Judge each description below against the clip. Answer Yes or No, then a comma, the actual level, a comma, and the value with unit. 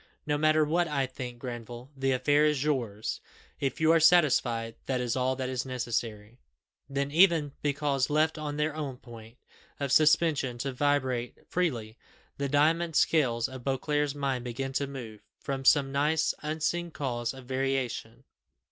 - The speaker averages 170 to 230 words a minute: No, average, 155 wpm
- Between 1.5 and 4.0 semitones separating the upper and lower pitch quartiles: Yes, average, 3.2 semitones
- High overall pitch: No, low, 135 Hz